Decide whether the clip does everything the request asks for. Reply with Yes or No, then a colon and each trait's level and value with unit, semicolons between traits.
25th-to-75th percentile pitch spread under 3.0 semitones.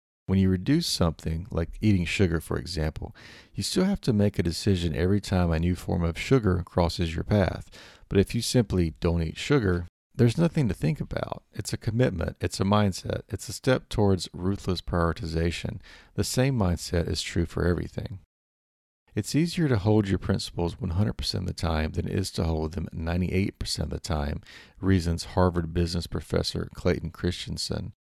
No: average, 3.9 semitones